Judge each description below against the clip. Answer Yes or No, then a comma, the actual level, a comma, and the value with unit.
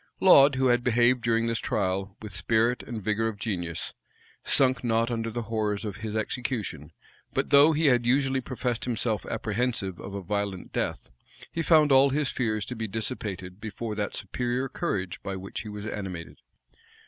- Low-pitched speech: Yes, low, 115 Hz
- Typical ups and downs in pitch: Yes, average, 3.6 semitones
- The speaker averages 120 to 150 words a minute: No, average, 175 wpm